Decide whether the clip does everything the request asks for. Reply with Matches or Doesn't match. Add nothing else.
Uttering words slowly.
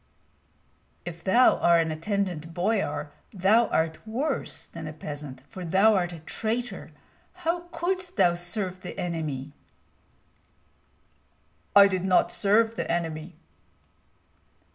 Matches